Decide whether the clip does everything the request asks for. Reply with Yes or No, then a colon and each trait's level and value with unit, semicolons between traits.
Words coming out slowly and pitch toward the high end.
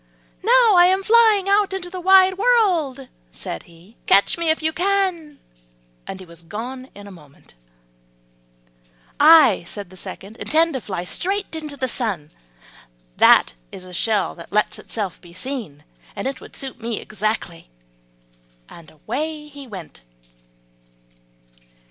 No: average, 145 wpm; very high, 265 Hz